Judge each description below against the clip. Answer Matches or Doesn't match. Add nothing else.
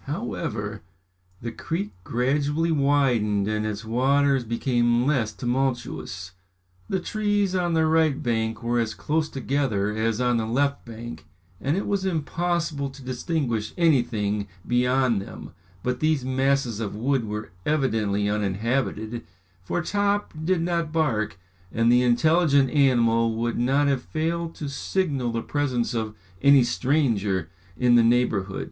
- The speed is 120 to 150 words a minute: Matches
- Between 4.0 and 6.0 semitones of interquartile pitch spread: Matches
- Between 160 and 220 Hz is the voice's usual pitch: Doesn't match